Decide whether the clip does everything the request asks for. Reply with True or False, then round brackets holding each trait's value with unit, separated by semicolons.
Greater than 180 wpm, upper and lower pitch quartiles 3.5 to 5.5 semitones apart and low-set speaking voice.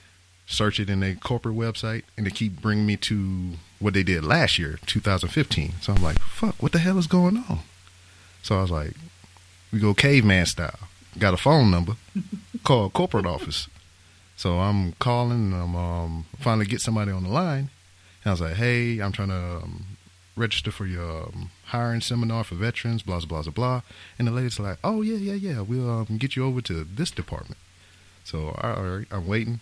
True (200 wpm; 4.7 semitones; 100 Hz)